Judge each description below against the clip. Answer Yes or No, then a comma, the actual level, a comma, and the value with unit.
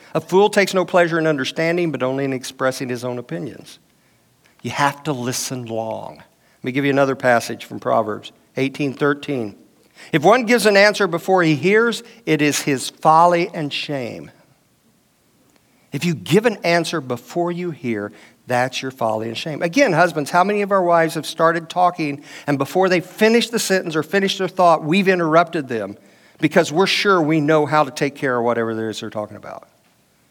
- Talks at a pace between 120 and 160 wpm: No, average, 185 wpm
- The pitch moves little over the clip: No, average, 5.2 semitones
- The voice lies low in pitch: No, medium, 155 Hz